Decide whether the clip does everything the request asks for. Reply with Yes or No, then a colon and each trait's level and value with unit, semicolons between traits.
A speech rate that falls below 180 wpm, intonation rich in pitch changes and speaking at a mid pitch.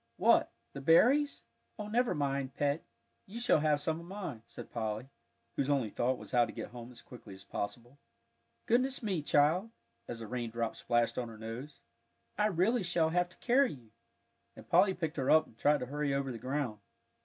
No: average, 195 wpm; wide, 6.8 semitones; medium, 145 Hz